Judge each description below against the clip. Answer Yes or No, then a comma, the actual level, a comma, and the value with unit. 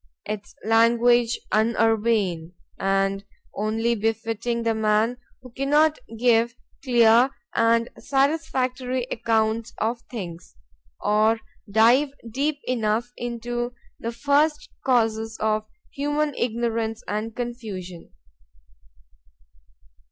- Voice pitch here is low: No, high, 230 Hz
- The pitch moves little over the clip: Yes, narrow, 2.0 semitones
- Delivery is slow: Yes, slow, 85 wpm